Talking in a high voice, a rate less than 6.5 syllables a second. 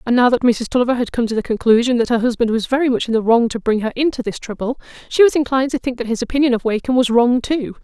No: high, 240 Hz; 7.0 syllables/s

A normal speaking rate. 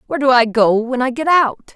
No: fast, 275 wpm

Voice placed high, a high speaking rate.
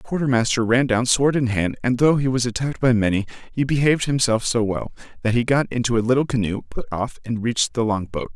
No: low, 120 Hz; fast, 245 wpm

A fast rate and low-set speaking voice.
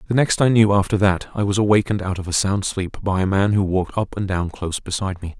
Yes: fast, 280 wpm; low, 100 Hz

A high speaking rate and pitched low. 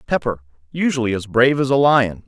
No: average, 185 wpm; low, 120 Hz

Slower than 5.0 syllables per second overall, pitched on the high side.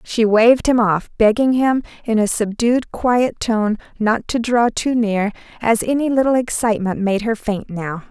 Yes: 4.5 syllables/s; high, 225 Hz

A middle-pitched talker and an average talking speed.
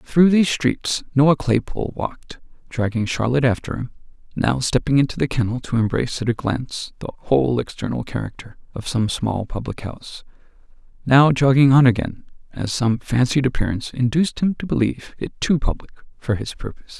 No: low, 125 Hz; average, 165 wpm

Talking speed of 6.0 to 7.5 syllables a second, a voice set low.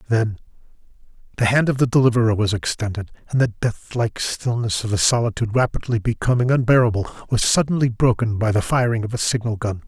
Yes: 6.1 syllables/s; low, 115 Hz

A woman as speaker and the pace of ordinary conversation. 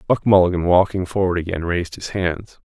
No: male; average, 180 wpm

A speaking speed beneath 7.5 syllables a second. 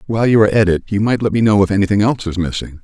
No: 8.0 syllables/s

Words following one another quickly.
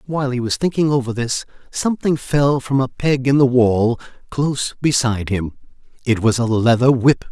No: average, 180 wpm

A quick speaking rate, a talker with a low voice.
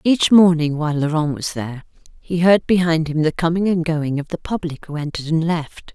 No: fast, 210 wpm; medium, 160 Hz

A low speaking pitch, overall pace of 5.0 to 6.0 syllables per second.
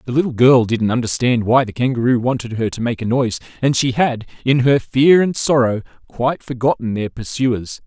Yes: low, 125 Hz; 5.4 syllables/s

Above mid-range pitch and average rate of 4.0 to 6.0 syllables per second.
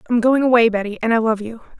No: high, 230 Hz; 6.9 syllables/s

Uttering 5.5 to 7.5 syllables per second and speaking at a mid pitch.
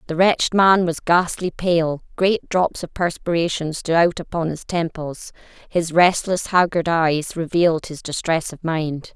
No: 4.2 syllables/s; medium, 170 Hz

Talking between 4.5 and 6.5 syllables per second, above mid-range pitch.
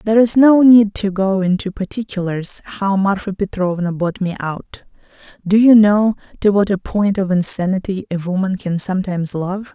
Yes: 4.9 syllables/s; high, 195 Hz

